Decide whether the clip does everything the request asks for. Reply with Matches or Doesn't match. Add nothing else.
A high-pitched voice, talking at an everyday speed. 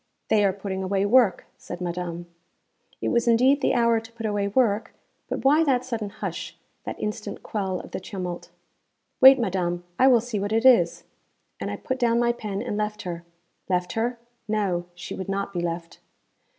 Matches